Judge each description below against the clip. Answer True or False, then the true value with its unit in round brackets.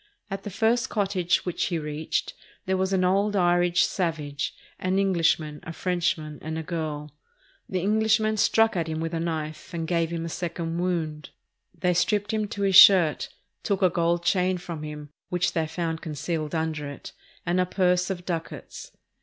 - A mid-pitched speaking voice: True (175 Hz)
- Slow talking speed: False (180 wpm)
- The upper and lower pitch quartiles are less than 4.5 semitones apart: True (2.8 semitones)